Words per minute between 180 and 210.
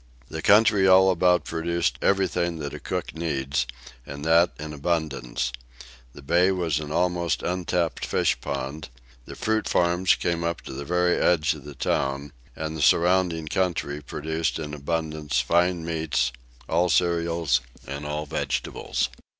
No: average, 150 wpm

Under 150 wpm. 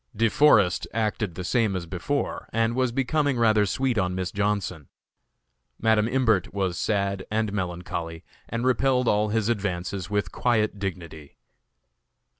Yes: average, 140 wpm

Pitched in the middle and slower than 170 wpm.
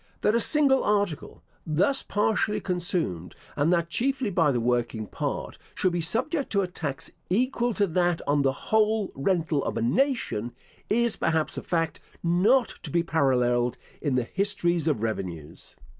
Yes: medium, 175 Hz; average, 160 wpm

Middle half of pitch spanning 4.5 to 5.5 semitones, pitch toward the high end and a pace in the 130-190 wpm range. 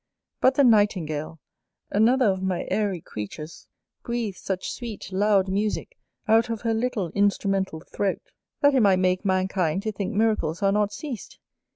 No: average, 3.1 semitones; high, 200 Hz; average, 155 wpm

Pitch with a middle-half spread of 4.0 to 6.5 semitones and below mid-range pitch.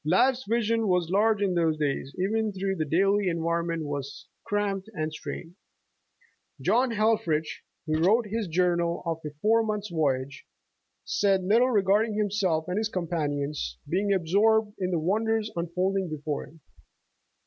No: average, 4.6 semitones; medium, 185 Hz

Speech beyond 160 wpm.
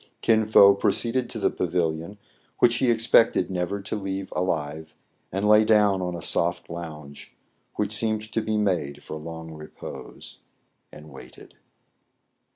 No: average, 150 wpm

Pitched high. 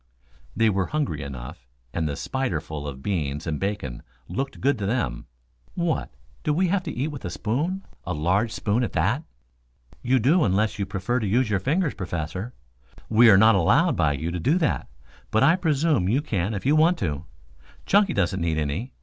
No: low, 105 Hz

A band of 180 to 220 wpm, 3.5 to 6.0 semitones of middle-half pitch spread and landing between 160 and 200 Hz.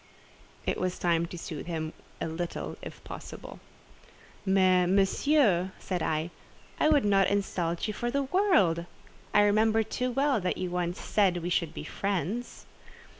No: average, 155 wpm; average, 4.1 semitones; high, 190 Hz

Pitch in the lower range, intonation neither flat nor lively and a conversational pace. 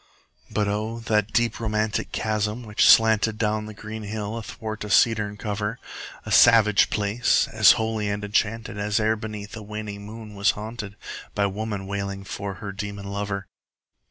No: low, 105 Hz; narrow, 1.3 semitones; average, 165 wpm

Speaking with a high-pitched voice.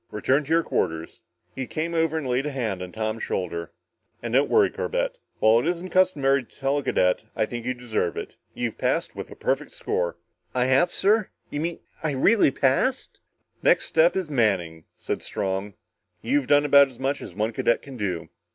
No: low, 130 Hz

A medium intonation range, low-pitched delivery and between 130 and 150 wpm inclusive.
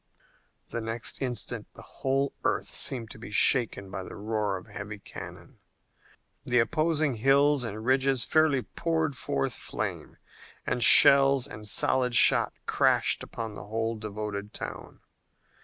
Yes: average, 4.2 semitones; low, 120 Hz; average, 140 wpm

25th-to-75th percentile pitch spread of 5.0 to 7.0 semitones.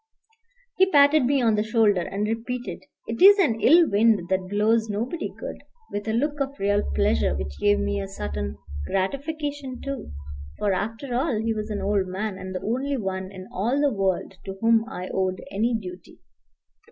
Yes: wide, 5.4 semitones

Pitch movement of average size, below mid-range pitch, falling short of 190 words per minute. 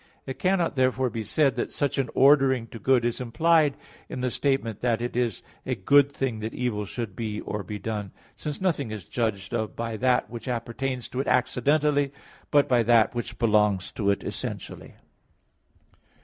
Yes: average, 3.6 semitones; low, 120 Hz; average, 180 wpm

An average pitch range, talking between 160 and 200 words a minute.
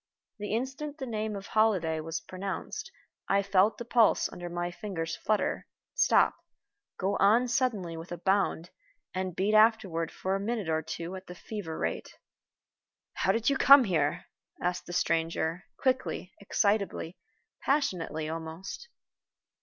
No: average, 4.7 semitones; average, 145 wpm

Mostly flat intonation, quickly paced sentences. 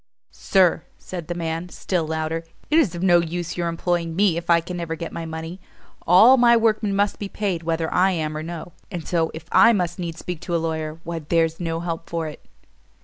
Yes: narrow, 1.8 semitones; fast, 220 wpm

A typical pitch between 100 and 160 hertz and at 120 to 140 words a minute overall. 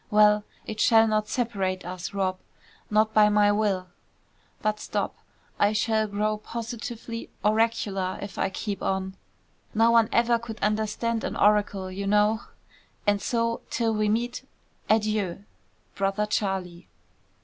No: high, 210 Hz; slow, 135 wpm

